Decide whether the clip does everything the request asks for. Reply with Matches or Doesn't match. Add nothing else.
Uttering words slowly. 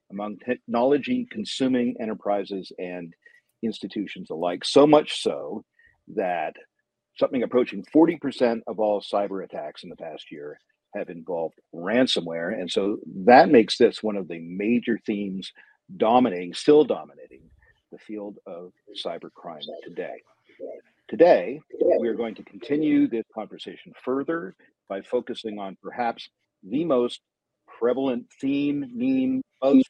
Matches